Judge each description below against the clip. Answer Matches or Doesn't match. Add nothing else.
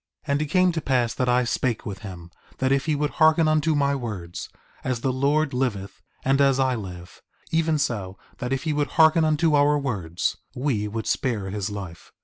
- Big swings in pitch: Matches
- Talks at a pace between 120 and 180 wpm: Doesn't match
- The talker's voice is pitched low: Matches